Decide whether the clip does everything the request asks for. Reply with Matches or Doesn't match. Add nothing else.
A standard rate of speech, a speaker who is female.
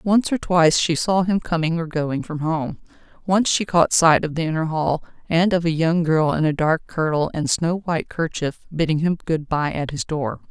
Doesn't match